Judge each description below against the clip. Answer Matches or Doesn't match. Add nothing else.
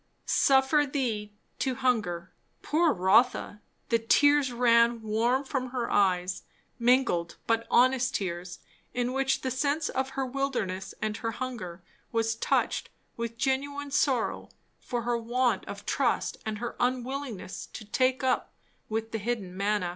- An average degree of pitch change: Matches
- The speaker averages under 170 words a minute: Matches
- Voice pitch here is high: Matches